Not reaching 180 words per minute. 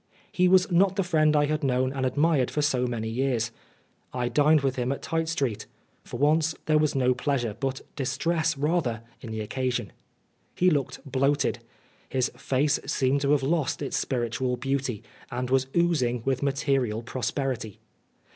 Yes: average, 165 wpm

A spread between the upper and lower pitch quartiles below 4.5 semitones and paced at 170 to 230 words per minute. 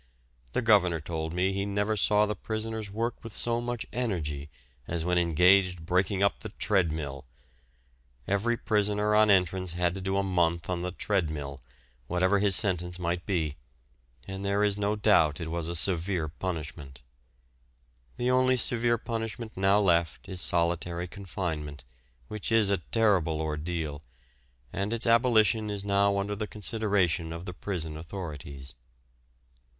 No: average, 3.8 semitones; average, 150 wpm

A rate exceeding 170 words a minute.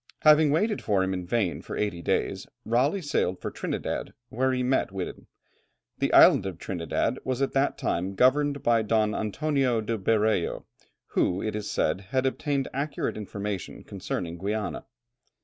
No: average, 160 wpm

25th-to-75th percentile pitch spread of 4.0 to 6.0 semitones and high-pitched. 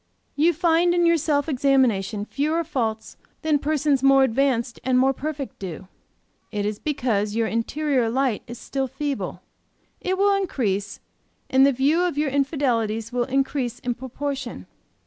Yes: average, 4.3 semitones; very high, 270 Hz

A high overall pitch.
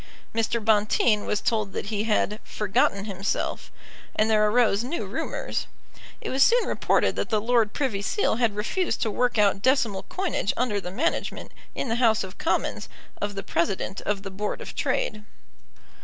Yes: high, 215 Hz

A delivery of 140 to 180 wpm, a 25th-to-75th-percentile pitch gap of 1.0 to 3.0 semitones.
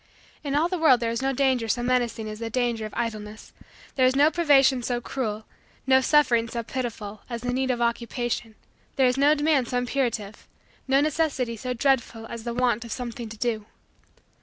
No: average, 195 wpm; narrow, 2.6 semitones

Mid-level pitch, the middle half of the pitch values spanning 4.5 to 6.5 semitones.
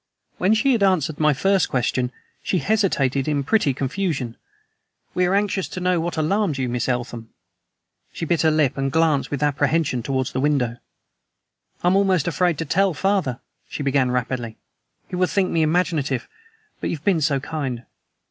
Yes: medium, 155 Hz; wide, 5.5 semitones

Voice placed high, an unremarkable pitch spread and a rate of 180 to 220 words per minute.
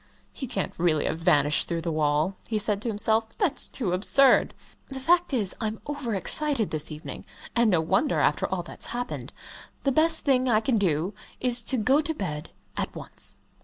No: high, 215 Hz; wide, 7.4 semitones; average, 190 wpm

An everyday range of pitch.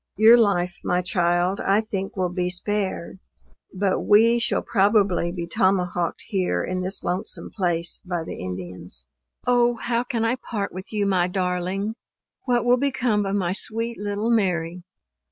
Yes: average, 3.6 semitones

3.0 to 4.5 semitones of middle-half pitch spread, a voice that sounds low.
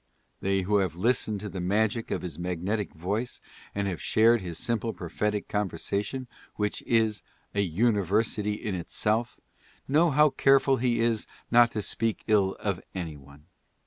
Yes: average, 3.6 semitones; low, 105 Hz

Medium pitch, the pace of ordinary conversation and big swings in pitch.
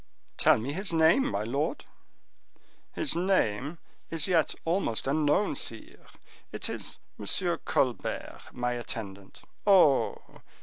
No: medium, 150 Hz; slow, 115 wpm; wide, 6.9 semitones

